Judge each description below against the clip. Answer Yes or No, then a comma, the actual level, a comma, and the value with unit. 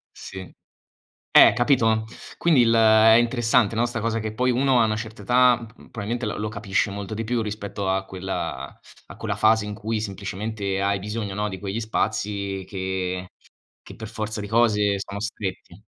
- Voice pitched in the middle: No, low, 110 Hz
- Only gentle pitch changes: Yes, narrow, 2.3 semitones